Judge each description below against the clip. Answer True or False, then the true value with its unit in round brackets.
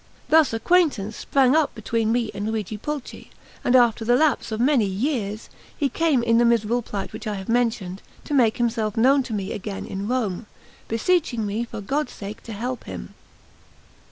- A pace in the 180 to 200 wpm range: True (185 wpm)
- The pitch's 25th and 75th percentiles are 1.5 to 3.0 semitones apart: False (3.4 semitones)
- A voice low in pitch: False (230 Hz)